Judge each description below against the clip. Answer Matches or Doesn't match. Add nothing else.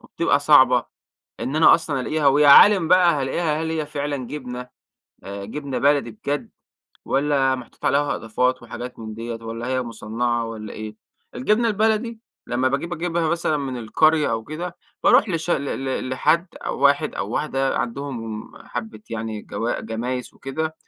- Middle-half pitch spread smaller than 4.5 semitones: Doesn't match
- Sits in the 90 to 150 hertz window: Matches